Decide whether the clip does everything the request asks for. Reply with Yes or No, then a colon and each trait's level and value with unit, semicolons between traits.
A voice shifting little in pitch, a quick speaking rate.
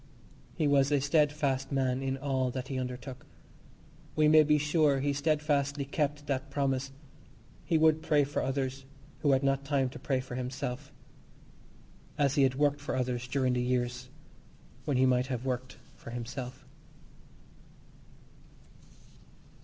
No: narrow, 2.0 semitones; average, 145 wpm